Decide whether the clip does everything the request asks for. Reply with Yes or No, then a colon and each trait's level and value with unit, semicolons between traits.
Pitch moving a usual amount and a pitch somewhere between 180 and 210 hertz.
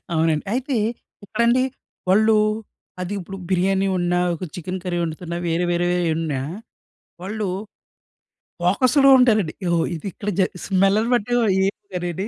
Yes: average, 3.6 semitones; medium, 185 Hz